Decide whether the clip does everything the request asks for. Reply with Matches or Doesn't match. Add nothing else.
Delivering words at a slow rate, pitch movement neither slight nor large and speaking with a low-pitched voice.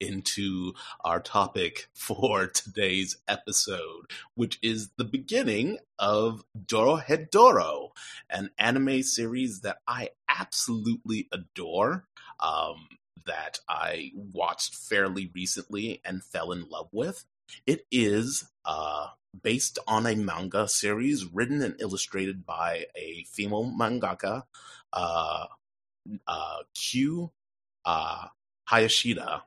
Matches